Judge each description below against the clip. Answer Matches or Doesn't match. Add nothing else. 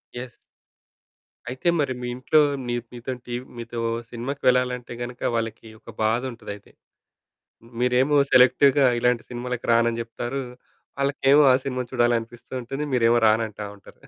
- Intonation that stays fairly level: Matches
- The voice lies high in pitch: Doesn't match